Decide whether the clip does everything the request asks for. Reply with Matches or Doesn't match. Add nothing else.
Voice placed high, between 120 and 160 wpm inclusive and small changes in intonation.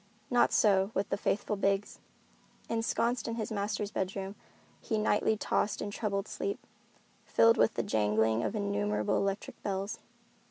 Matches